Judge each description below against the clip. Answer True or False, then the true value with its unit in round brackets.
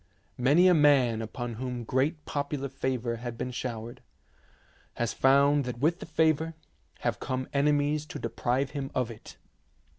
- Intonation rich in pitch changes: False (3.3 semitones)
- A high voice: False (130 Hz)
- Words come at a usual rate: True (150 wpm)